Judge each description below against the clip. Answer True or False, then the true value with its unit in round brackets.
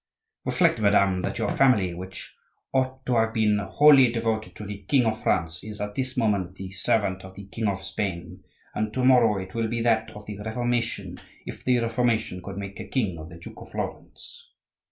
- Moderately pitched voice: False (105 Hz)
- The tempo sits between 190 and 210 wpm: True (200 wpm)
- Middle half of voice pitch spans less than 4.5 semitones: True (3.5 semitones)